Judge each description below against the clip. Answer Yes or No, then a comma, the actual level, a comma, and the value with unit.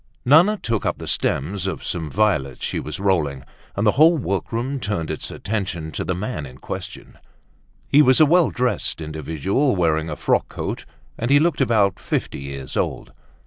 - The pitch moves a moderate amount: No, wide, 8.5 semitones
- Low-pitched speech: Yes, low, 100 Hz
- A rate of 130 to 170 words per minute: No, average, 180 wpm